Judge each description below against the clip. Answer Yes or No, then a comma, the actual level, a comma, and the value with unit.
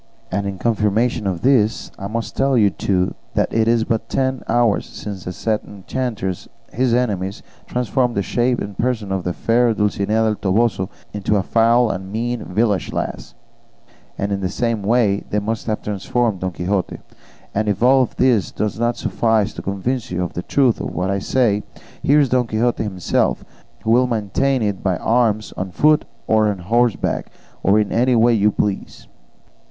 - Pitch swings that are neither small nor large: Yes, average, 3.3 semitones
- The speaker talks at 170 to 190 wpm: Yes, average, 180 wpm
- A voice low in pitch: Yes, low, 110 Hz